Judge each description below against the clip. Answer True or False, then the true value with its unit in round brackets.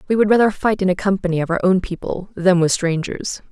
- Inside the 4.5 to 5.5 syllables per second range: False (6.0 syllables/s)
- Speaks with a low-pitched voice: False (190 Hz)